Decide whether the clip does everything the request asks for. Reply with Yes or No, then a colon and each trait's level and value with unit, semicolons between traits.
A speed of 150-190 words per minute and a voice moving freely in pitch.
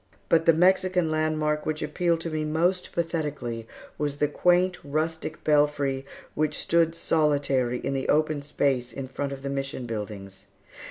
No: average, 155 wpm; average, 3.0 semitones